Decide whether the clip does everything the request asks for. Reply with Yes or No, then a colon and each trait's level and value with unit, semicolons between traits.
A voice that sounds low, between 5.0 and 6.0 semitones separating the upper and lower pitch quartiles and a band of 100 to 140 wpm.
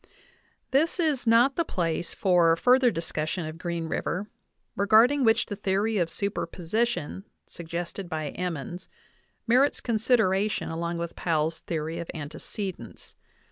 No: medium, 185 Hz; average, 5.3 semitones; slow, 135 wpm